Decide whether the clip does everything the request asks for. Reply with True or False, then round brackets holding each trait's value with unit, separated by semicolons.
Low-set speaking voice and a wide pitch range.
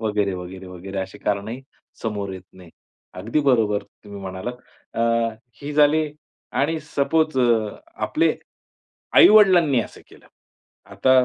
True (110 Hz; 6.5 semitones)